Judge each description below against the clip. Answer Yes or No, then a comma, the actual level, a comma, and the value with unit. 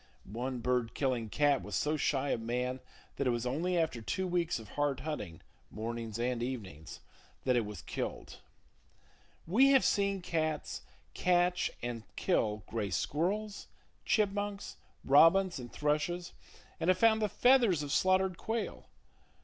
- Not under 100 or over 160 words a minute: Yes, average, 145 wpm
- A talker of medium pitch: Yes, medium, 150 Hz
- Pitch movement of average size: No, wide, 7.3 semitones